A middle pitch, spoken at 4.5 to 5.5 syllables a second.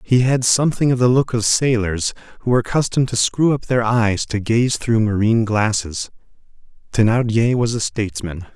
No: low, 115 Hz; 5.4 syllables/s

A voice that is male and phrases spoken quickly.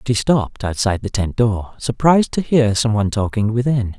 Yes: male; fast, 210 wpm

